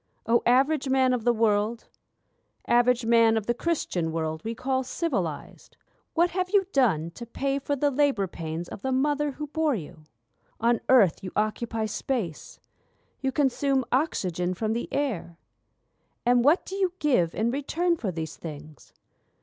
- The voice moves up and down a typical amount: No, wide, 6.3 semitones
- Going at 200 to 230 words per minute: No, average, 160 wpm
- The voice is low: No, high, 240 Hz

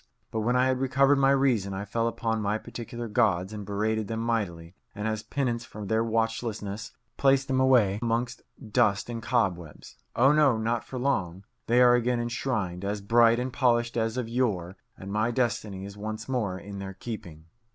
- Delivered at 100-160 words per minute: No, average, 185 wpm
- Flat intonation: No, average, 3.3 semitones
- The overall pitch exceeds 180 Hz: No, low, 115 Hz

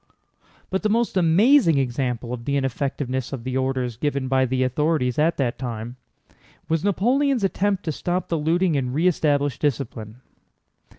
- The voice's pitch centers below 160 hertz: Yes, medium, 140 Hz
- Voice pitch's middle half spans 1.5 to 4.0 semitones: No, wide, 5.4 semitones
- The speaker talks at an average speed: Yes, average, 160 wpm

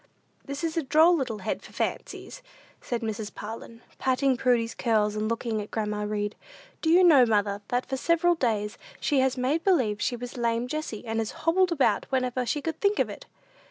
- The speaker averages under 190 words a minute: No, average, 195 wpm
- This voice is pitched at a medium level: No, high, 245 Hz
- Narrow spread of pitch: No, wide, 5.6 semitones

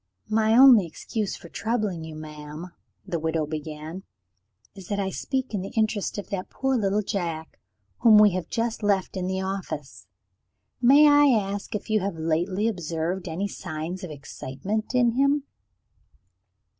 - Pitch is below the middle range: No, high, 195 Hz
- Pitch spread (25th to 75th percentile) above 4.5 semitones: Yes, average, 5.0 semitones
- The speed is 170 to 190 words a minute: No, average, 155 wpm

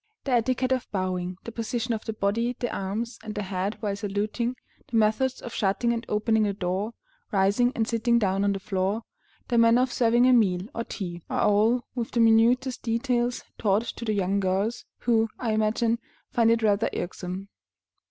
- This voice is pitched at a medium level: No, high, 220 Hz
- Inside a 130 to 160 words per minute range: No, average, 190 wpm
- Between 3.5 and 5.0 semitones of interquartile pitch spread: No, average, 2.9 semitones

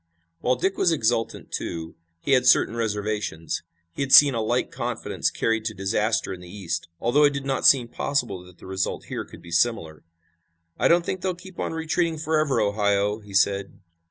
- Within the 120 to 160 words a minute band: No, average, 190 wpm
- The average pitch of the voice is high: No, low, 115 Hz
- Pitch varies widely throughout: Yes, wide, 6.3 semitones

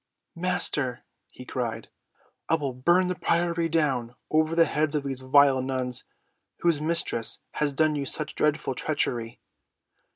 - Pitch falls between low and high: Yes, medium, 145 Hz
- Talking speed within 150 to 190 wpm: No, average, 140 wpm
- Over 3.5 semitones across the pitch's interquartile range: Yes, average, 4.0 semitones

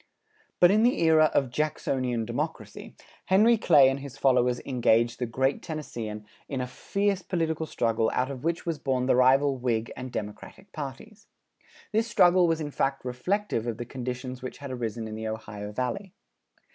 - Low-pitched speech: Yes, low, 130 Hz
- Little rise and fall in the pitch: No, average, 5.1 semitones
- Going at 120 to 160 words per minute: No, average, 170 wpm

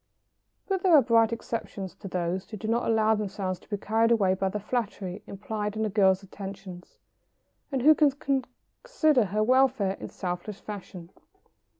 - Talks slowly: No, average, 175 wpm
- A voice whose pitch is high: Yes, high, 210 Hz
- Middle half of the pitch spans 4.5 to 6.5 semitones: No, average, 3.6 semitones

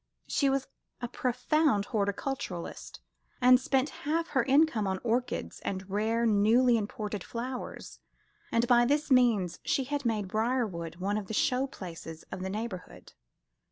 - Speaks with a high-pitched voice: Yes, high, 230 Hz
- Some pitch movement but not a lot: Yes, average, 4.4 semitones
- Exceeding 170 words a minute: No, average, 145 wpm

